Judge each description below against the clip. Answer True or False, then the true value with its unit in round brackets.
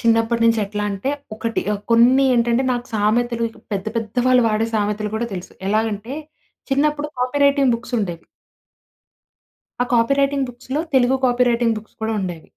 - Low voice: False (235 Hz)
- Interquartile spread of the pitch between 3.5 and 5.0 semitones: False (2.9 semitones)